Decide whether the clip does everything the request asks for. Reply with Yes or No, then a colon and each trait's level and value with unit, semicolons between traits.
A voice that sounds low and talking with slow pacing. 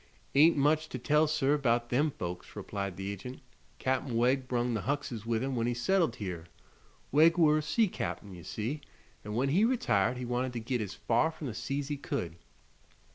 No: low, 125 Hz; average, 200 wpm